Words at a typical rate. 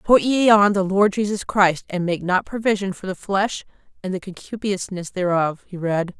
Yes: average, 195 wpm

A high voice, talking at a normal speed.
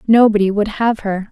Yes: high, 210 Hz; average, 185 wpm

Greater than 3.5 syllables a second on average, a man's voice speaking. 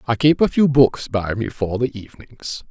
Yes: 4.8 syllables/s; male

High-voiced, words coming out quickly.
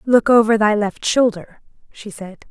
No: high, 215 Hz; average, 170 wpm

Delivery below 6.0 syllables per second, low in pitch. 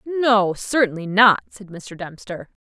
No: 4.0 syllables/s; high, 205 Hz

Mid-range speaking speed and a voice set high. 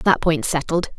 No: average, 185 wpm; medium, 160 Hz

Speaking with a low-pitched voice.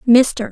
No: high, 240 Hz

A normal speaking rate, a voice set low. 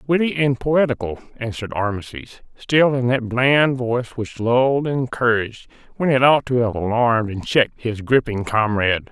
Yes: average, 165 wpm; low, 120 Hz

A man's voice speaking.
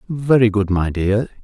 Yes: male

